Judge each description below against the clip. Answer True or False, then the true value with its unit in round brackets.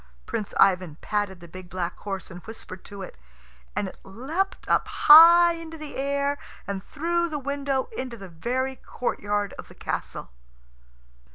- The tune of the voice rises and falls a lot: True (7.0 semitones)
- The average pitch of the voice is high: True (235 Hz)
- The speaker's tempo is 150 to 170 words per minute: True (160 wpm)